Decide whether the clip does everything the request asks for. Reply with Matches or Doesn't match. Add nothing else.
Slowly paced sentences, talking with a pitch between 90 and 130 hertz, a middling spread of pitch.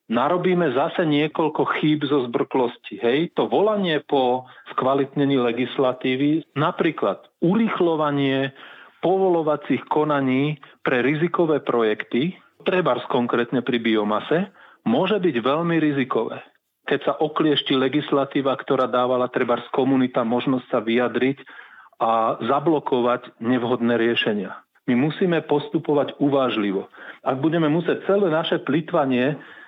Doesn't match